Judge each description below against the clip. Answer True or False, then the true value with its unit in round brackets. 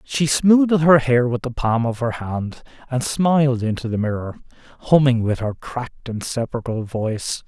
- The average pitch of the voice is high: False (125 Hz)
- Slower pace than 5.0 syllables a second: True (4.8 syllables/s)